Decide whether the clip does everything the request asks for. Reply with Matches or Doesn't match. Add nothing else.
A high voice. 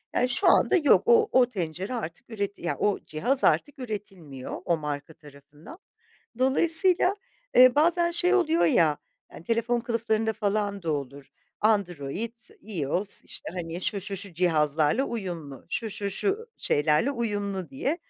Matches